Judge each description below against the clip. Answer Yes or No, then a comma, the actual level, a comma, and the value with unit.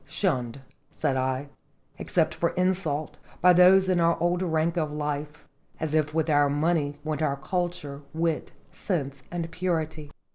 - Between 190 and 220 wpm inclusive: No, average, 150 wpm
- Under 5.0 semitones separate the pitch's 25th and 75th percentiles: Yes, average, 3.1 semitones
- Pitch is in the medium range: Yes, medium, 155 Hz